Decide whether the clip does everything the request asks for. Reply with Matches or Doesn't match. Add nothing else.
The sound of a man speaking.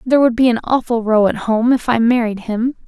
Doesn't match